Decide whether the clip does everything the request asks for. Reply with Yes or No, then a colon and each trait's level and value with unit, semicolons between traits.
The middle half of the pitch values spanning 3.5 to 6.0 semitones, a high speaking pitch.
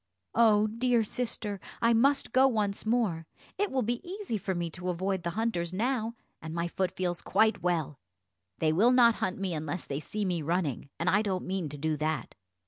Yes: average, 5.1 semitones; high, 195 Hz